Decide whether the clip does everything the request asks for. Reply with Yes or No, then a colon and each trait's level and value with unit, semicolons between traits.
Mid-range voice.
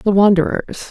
No: high, 195 Hz